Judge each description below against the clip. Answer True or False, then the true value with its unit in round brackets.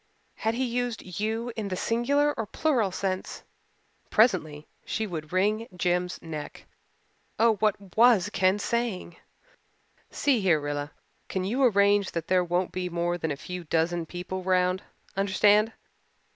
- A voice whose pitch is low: False (190 Hz)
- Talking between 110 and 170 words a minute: True (145 wpm)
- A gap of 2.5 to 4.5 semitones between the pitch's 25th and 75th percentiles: True (4.0 semitones)